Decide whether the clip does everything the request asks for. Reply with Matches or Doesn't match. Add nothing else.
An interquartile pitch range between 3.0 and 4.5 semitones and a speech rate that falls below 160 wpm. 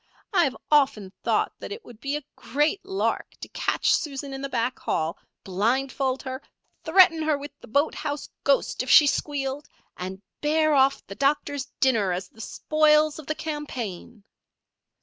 Doesn't match